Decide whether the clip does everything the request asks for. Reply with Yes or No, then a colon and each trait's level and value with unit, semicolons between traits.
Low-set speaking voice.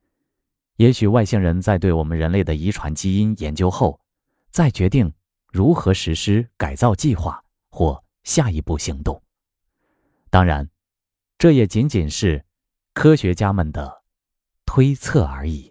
Yes: very low, 95 Hz